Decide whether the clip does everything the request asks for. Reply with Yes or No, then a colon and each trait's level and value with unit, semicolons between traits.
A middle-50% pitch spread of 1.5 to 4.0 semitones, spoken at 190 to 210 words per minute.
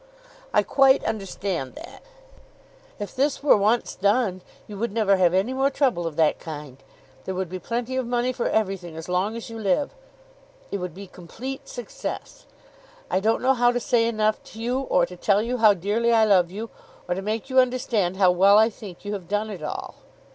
No: average, 4.4 semitones; fast, 205 wpm